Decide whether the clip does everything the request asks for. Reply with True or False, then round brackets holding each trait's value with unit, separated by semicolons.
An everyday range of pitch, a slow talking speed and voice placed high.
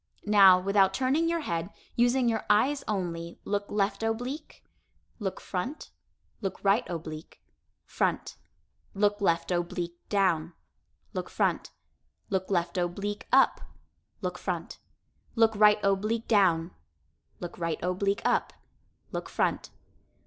True (3.9 semitones; 120 wpm; 200 Hz)